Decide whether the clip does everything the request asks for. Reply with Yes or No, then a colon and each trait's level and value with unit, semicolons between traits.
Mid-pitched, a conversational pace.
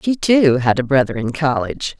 No: medium, 145 Hz; fast, 210 wpm